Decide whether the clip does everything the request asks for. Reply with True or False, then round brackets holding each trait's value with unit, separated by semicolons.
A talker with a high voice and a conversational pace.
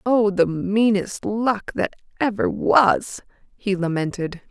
False (205 Hz; 120 wpm)